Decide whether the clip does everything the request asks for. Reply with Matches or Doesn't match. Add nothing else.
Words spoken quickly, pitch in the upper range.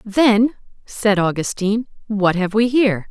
Doesn't match